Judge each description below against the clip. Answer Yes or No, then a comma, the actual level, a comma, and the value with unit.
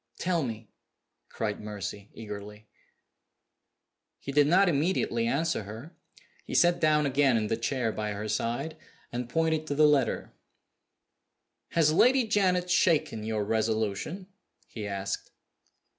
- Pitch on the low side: Yes, low, 125 Hz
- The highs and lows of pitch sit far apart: Yes, wide, 6.9 semitones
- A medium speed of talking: No, slow, 130 wpm